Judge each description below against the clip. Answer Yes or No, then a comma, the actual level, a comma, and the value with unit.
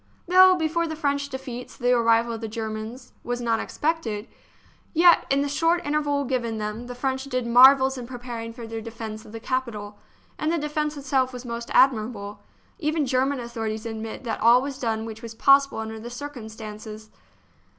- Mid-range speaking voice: No, high, 245 Hz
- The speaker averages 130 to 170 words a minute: No, average, 180 wpm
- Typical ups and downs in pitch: Yes, average, 3.8 semitones